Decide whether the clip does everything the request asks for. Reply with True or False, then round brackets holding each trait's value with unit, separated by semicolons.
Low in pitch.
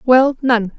False (245 Hz)